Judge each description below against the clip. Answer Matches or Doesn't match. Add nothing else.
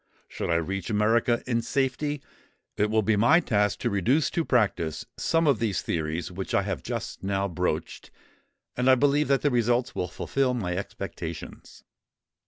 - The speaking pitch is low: Matches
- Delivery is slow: Doesn't match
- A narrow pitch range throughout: Doesn't match